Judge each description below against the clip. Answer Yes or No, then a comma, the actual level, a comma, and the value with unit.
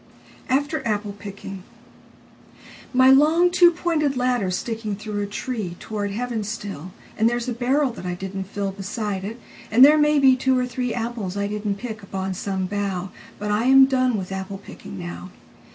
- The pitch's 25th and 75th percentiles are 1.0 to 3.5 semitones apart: No, average, 4.6 semitones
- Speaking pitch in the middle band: No, high, 215 Hz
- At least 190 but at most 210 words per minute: No, average, 165 wpm